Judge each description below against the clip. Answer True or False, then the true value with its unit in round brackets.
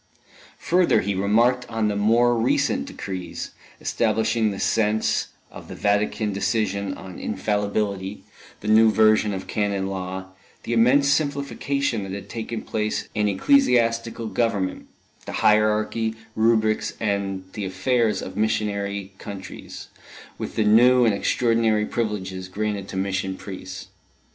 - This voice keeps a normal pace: False (130 wpm)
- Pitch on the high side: False (105 Hz)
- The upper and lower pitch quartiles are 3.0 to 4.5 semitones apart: False (2.5 semitones)